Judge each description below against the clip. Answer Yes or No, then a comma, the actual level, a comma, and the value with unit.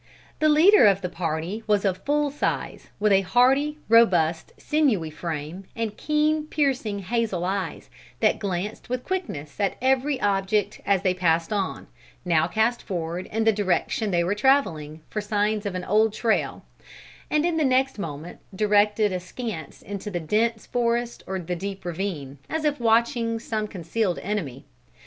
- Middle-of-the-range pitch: No, high, 205 Hz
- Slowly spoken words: No, average, 160 wpm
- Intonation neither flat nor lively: Yes, average, 4.8 semitones